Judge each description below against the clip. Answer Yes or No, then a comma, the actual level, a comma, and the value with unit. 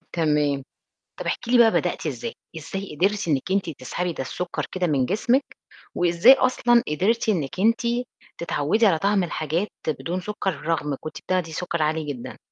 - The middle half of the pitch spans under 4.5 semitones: No, average, 5.3 semitones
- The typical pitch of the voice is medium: Yes, medium, 175 Hz